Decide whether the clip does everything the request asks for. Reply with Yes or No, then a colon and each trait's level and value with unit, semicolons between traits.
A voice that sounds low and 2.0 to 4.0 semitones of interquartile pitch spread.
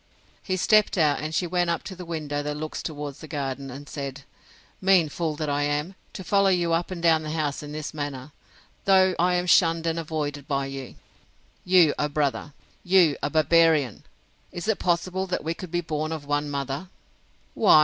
No: medium, 155 Hz; average, 3.2 semitones